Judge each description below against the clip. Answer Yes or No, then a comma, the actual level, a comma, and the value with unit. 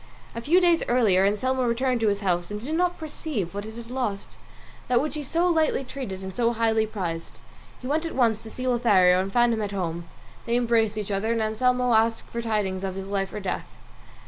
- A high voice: Yes, high, 225 Hz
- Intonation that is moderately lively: Yes, average, 4.2 semitones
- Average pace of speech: No, fast, 230 wpm